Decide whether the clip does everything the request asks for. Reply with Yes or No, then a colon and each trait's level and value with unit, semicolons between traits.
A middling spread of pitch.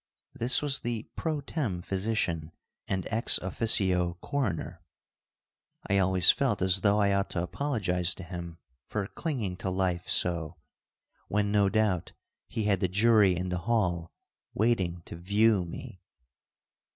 Yes: average, 3.7 semitones